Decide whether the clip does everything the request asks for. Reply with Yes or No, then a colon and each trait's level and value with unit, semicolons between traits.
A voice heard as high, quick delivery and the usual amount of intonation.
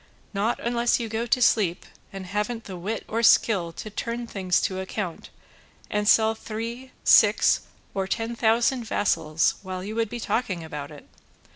No: high, 215 Hz; average, 165 wpm; average, 3.7 semitones